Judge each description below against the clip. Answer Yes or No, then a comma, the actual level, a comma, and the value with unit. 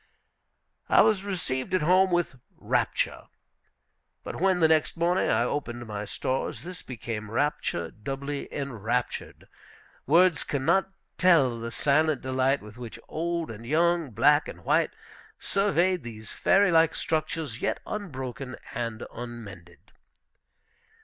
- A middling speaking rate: No, slow, 130 wpm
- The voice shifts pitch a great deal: Yes, wide, 6.3 semitones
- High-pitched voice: No, medium, 140 Hz